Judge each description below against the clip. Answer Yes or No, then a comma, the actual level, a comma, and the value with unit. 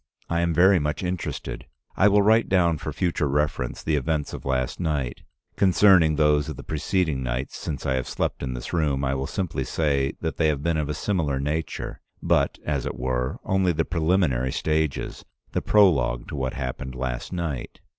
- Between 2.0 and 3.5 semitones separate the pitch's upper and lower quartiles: No, average, 4.2 semitones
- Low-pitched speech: Yes, very low, 75 Hz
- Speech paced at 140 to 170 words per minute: No, average, 190 wpm